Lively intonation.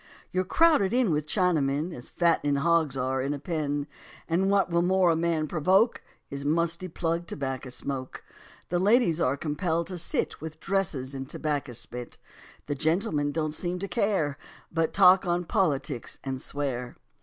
No: average, 4.2 semitones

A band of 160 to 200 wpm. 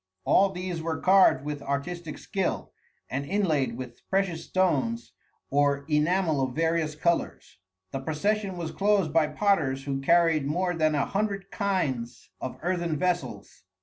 No: average, 145 wpm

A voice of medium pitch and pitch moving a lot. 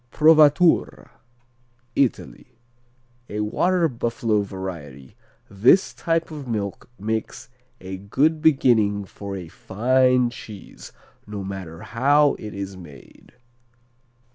No: low, 110 Hz; wide, 6.0 semitones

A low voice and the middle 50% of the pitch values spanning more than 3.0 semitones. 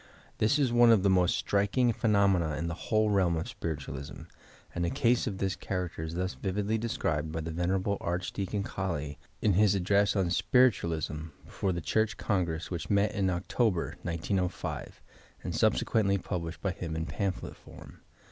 Yes: very low, 95 Hz; average, 3.5 semitones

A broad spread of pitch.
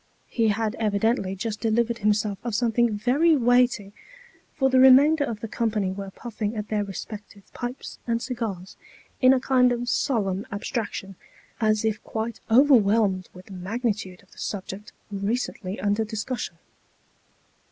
No: average, 3.2 semitones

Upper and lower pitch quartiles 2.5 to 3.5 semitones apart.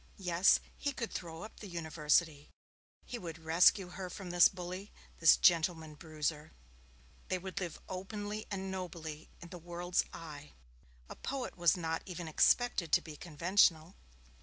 Yes: average, 2.8 semitones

